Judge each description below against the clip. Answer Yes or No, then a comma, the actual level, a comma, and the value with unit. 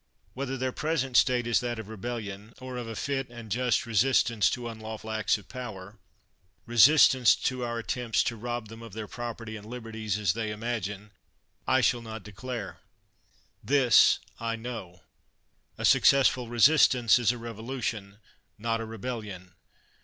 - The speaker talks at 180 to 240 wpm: No, average, 160 wpm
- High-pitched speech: No, low, 115 Hz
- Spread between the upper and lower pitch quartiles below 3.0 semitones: Yes, narrow, 2.4 semitones